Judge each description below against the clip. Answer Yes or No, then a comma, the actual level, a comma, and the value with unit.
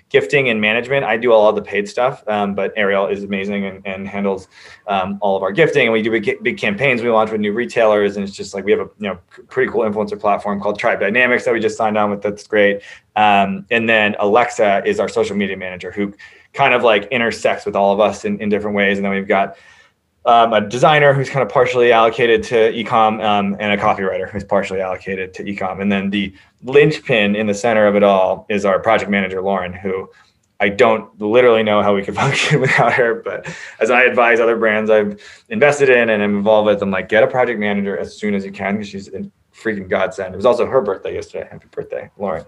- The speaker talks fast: Yes, fast, 235 wpm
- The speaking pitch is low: Yes, low, 105 Hz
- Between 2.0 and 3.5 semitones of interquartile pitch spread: Yes, average, 3.2 semitones